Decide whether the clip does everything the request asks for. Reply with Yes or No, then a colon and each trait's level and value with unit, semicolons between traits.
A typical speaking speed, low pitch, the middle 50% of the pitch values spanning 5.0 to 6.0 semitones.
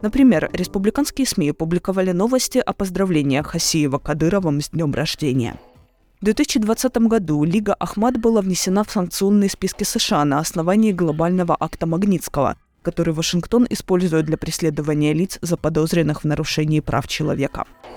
No: average, 130 wpm; medium, 175 Hz; average, 5.3 semitones